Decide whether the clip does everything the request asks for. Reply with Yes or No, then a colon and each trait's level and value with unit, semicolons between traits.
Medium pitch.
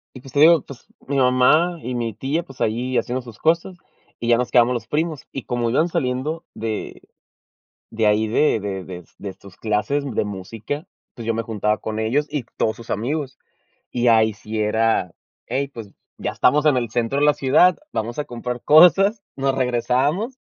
No: low, 125 Hz